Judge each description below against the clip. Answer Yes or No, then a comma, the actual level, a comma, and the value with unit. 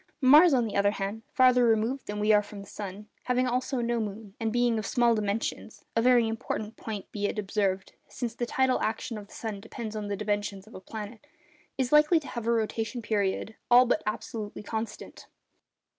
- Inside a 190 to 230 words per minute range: Yes, fast, 205 wpm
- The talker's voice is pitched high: Yes, high, 220 Hz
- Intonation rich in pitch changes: No, average, 2.7 semitones